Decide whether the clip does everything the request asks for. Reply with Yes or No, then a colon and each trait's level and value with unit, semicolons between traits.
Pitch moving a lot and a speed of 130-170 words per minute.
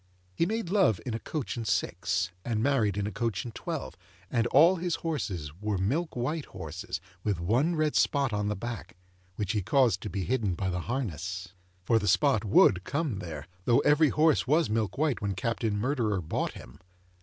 No: wide, 6.5 semitones; average, 195 wpm